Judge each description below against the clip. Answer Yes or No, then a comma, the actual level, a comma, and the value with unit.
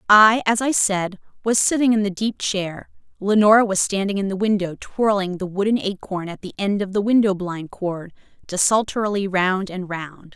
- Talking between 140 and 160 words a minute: No, average, 185 wpm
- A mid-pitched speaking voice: No, high, 200 Hz